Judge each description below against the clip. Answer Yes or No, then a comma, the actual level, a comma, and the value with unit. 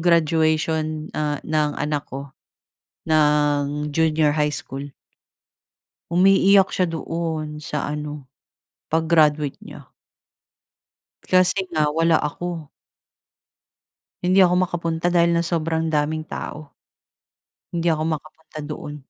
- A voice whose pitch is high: No, medium, 155 Hz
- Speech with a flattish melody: Yes, narrow, 2.0 semitones